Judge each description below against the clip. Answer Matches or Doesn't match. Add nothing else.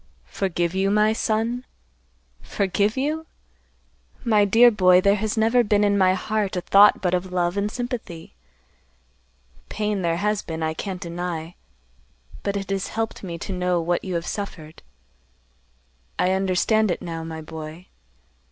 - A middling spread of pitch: Matches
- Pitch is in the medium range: Doesn't match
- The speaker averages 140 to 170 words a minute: Matches